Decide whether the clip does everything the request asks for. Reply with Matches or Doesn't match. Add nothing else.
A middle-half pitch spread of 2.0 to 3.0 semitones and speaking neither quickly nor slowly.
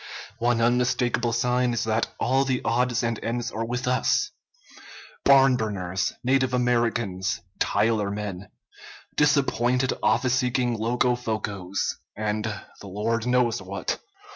Doesn't match